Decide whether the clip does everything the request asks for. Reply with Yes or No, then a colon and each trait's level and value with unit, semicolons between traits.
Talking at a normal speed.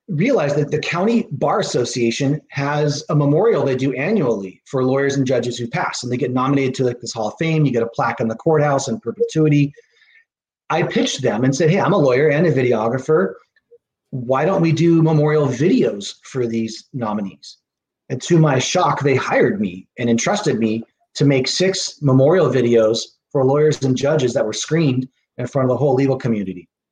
Yes: average, 195 wpm